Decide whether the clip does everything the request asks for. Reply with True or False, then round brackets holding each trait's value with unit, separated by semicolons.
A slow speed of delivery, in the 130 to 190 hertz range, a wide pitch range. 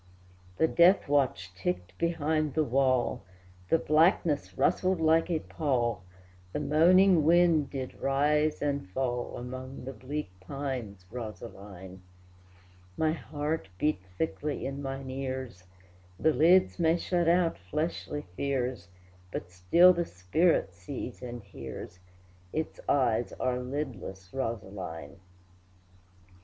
True (115 wpm; 135 Hz; 6.5 semitones)